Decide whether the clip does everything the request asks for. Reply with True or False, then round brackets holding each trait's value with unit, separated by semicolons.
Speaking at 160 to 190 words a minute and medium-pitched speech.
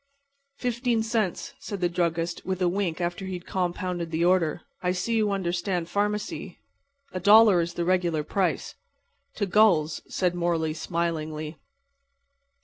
False (140 wpm; 180 Hz)